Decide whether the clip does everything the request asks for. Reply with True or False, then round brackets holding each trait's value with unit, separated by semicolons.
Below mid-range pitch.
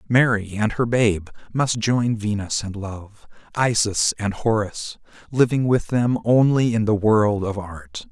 True (110 Hz)